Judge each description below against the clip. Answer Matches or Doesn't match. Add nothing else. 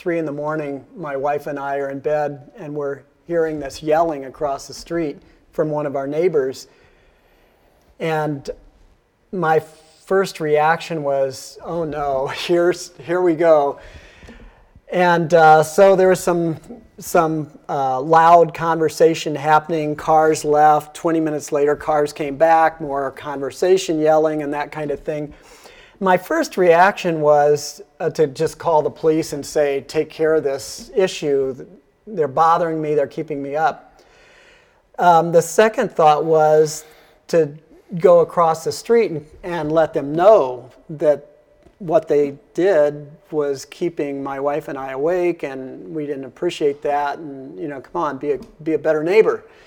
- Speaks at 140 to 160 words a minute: Matches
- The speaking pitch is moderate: Matches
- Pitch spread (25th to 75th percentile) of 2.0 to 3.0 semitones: Matches